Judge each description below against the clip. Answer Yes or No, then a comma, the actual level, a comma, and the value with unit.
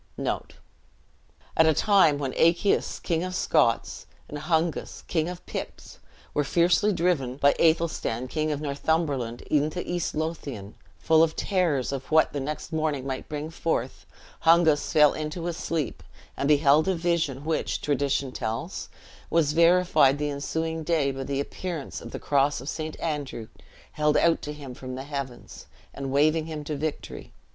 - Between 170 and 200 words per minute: No, average, 160 wpm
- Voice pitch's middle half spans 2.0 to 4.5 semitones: Yes, average, 2.9 semitones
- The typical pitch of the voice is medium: Yes, medium, 150 Hz